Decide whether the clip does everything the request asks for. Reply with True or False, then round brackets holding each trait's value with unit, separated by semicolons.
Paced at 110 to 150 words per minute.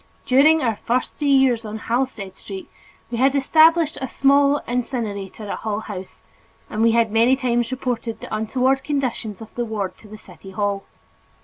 False (175 wpm)